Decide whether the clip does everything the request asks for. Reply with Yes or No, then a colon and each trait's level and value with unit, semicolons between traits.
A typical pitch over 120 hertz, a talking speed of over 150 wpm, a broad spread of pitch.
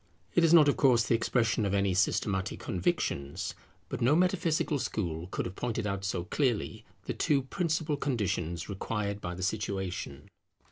No: low, 105 Hz; average, 160 wpm; wide, 6.5 semitones